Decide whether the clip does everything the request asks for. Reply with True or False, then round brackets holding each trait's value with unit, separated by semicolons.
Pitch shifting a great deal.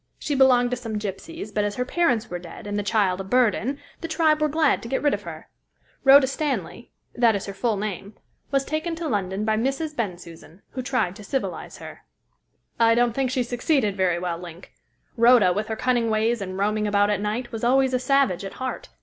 False (4.7 semitones)